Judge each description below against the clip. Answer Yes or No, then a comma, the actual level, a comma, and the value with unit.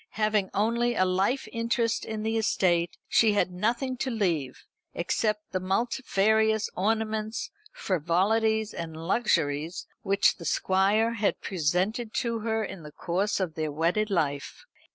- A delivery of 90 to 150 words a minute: Yes, slow, 135 wpm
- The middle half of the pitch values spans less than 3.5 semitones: No, average, 3.8 semitones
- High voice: Yes, high, 205 Hz